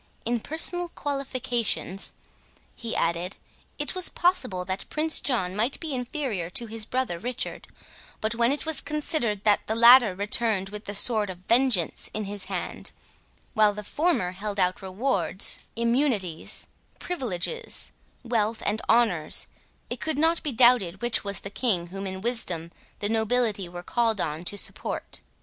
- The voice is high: Yes, high, 220 Hz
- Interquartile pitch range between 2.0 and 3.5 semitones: No, average, 4.7 semitones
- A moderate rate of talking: Yes, average, 155 wpm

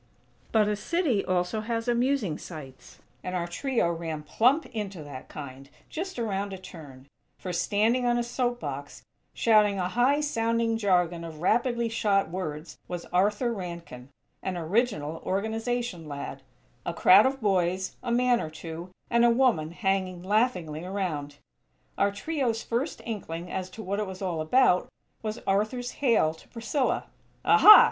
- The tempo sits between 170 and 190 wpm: No, average, 155 wpm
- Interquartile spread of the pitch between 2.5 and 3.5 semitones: No, wide, 5.6 semitones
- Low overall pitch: No, high, 200 Hz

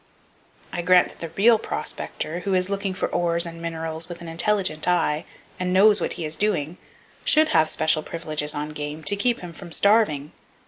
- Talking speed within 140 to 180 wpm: No, average, 190 wpm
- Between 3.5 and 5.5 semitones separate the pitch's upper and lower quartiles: Yes, average, 3.8 semitones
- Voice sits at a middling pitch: Yes, medium, 170 Hz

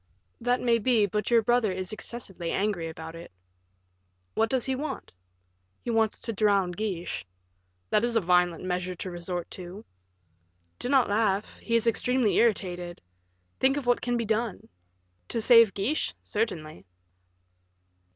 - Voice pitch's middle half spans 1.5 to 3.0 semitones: No, average, 4.6 semitones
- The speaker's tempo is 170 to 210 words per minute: No, average, 150 wpm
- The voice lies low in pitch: No, high, 215 Hz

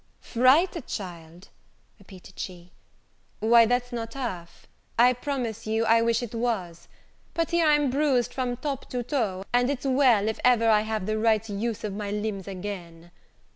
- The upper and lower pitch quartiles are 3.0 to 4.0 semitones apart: Yes, average, 3.7 semitones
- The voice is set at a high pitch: Yes, high, 225 Hz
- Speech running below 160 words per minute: No, average, 165 wpm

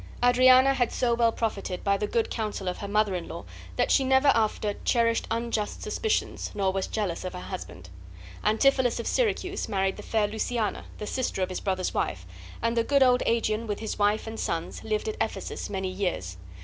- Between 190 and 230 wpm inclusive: Yes, average, 200 wpm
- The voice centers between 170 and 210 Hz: No, high, 220 Hz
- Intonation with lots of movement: No, average, 3.8 semitones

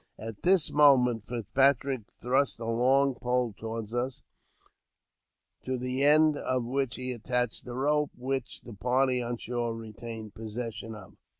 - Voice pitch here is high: No, low, 125 Hz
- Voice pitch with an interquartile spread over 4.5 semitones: No, average, 2.8 semitones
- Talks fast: No, average, 140 wpm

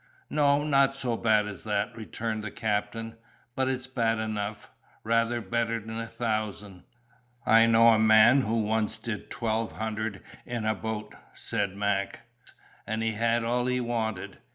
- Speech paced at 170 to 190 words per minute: No, average, 155 wpm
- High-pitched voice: No, low, 110 Hz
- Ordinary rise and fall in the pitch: No, narrow, 1.5 semitones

